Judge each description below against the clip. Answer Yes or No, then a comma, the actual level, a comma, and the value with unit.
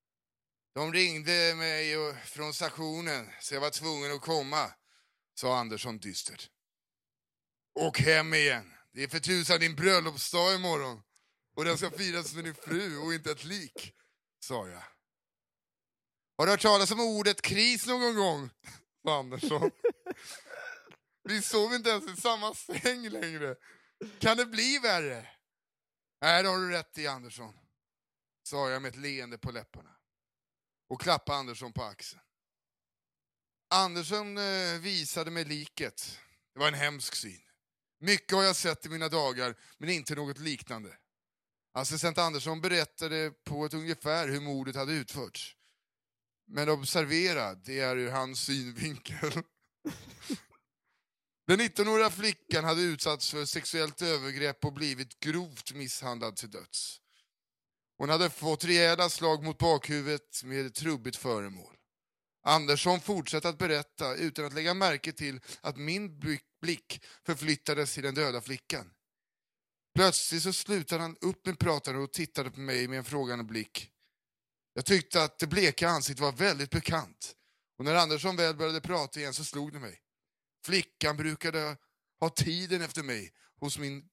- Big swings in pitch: No, average, 3.8 semitones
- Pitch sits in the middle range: Yes, medium, 155 Hz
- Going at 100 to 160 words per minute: Yes, average, 145 wpm